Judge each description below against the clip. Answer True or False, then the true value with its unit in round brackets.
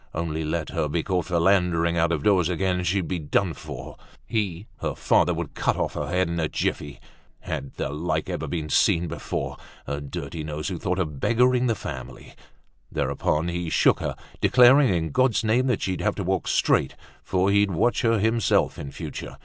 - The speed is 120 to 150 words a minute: False (190 wpm)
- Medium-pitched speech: False (90 Hz)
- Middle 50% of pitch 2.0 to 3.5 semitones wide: False (4.0 semitones)